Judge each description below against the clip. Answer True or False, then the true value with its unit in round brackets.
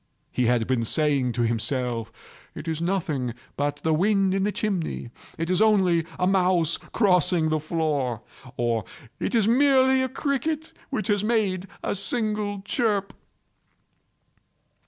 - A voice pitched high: False (180 Hz)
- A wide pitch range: True (6.6 semitones)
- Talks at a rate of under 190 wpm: True (135 wpm)